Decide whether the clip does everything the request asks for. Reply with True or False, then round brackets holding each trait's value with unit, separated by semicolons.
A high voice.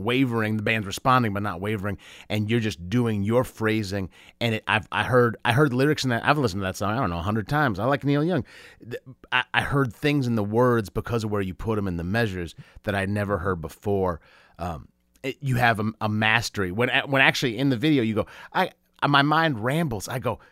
False (115 Hz)